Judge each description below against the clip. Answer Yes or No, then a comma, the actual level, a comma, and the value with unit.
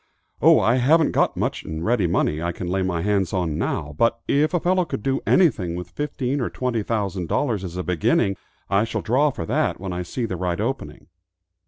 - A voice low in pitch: Yes, low, 100 Hz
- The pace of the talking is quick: Yes, fast, 215 wpm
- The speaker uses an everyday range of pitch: No, wide, 6.3 semitones